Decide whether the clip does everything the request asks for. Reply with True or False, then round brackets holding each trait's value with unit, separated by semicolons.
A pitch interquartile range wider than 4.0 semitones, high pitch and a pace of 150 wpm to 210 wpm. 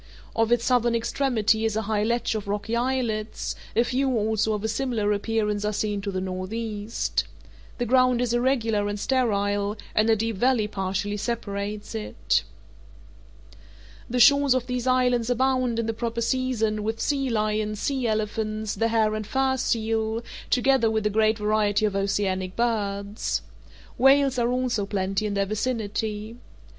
False (2.5 semitones; 220 Hz; 160 wpm)